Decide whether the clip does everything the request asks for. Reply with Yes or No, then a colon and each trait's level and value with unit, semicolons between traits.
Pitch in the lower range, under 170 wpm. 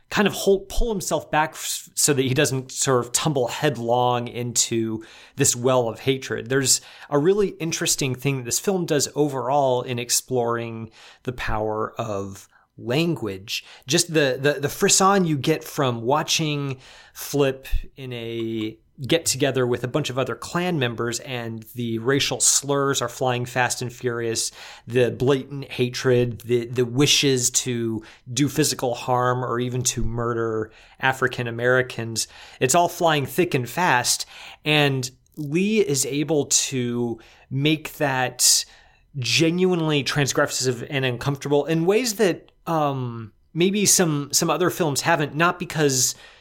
Yes: low, 130 Hz; average, 140 wpm